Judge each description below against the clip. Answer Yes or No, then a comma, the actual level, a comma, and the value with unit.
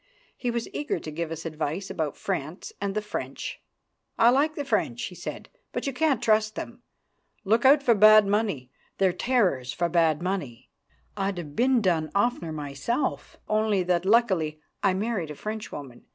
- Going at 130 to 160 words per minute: No, average, 170 wpm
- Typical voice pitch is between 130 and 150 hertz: No, high, 195 Hz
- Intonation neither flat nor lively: No, wide, 6.2 semitones